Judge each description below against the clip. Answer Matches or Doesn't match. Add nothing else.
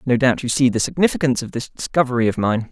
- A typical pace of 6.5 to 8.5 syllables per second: Matches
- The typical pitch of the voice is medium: Doesn't match